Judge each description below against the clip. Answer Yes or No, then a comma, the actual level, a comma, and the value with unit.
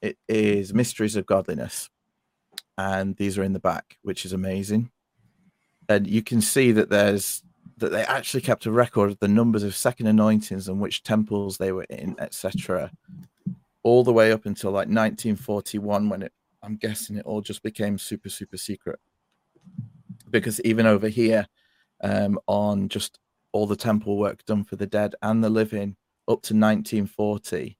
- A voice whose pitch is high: No, low, 105 Hz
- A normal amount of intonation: No, narrow, 1.5 semitones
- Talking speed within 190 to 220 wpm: No, average, 170 wpm